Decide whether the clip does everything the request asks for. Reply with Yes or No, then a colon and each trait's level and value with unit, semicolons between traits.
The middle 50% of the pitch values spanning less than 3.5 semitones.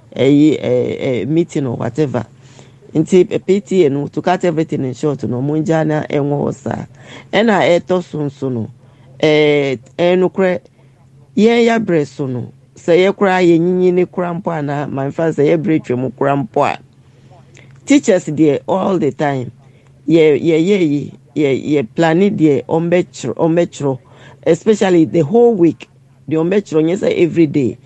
No: average, 4.3 semitones